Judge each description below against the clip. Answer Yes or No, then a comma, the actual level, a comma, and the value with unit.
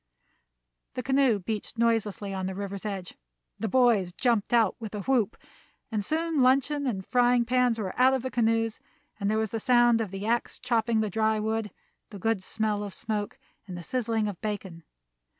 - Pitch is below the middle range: No, high, 220 Hz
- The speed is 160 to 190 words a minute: Yes, average, 185 wpm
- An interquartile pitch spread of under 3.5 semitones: Yes, average, 2.9 semitones